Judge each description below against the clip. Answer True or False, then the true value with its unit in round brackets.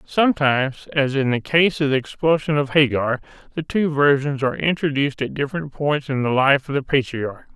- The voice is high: False (140 Hz)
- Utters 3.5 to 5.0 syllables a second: False (5.4 syllables/s)